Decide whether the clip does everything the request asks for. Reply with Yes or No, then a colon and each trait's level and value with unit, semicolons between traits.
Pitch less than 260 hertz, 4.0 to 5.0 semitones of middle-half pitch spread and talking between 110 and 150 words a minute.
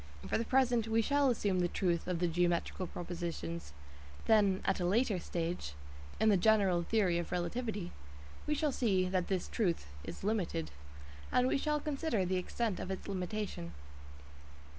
No: high, 190 Hz; average, 4.3 semitones; average, 160 wpm